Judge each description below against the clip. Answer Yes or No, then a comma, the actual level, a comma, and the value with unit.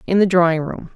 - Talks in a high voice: No, medium, 175 Hz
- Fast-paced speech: Yes, fast, 250 wpm